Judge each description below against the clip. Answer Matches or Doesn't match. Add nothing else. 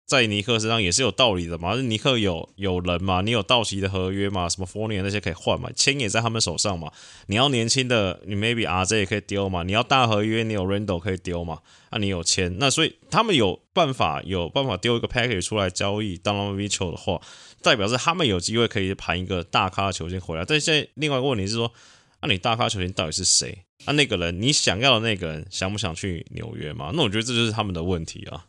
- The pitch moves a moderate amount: Matches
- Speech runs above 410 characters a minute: Matches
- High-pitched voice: Doesn't match